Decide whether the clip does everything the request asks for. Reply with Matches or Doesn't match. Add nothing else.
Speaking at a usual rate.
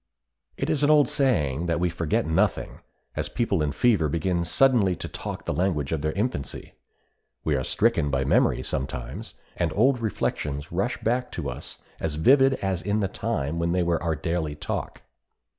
Matches